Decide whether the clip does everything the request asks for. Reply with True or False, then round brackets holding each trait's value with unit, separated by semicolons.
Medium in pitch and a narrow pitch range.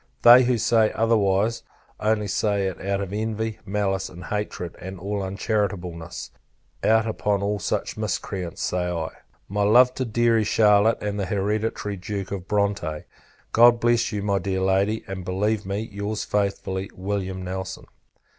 False (100 Hz; 2.2 semitones)